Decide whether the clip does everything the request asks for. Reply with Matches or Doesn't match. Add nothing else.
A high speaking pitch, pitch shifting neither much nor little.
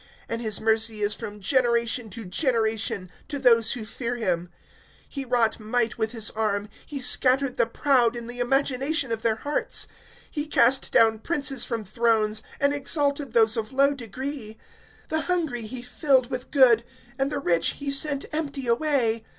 Matches